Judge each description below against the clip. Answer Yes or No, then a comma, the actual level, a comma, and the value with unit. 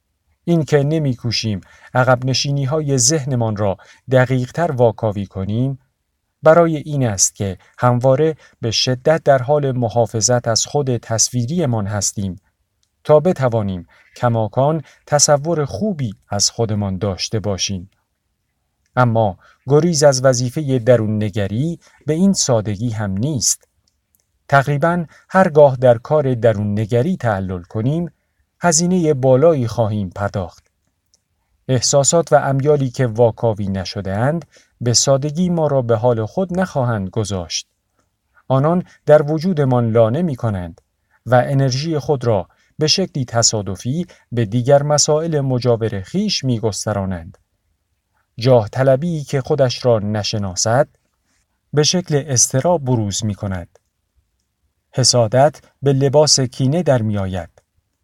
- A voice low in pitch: Yes, low, 125 Hz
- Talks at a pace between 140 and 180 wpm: No, average, 115 wpm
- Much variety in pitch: Yes, wide, 6.1 semitones